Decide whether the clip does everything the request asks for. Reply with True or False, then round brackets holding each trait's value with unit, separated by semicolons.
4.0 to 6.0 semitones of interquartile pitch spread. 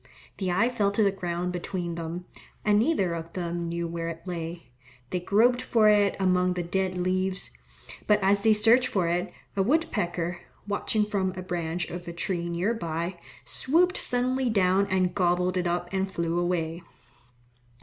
False (2.9 semitones)